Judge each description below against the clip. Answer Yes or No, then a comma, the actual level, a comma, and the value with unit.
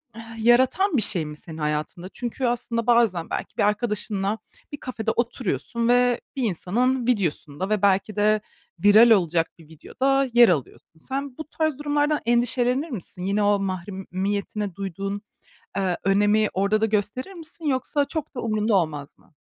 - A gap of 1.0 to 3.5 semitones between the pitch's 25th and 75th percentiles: No, average, 4.5 semitones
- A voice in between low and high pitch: No, high, 215 Hz